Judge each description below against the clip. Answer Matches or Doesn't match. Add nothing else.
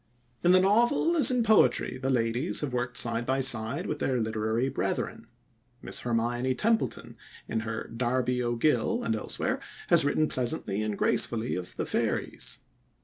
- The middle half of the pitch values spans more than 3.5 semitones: Matches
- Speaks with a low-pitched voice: Matches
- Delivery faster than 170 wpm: Doesn't match